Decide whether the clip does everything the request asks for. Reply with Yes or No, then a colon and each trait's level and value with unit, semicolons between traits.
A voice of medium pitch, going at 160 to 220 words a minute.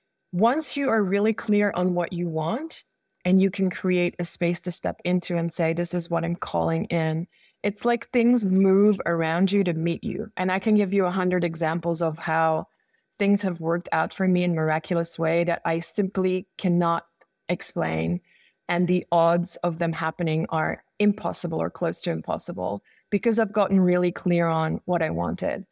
Yes: medium, 175 Hz; average, 190 wpm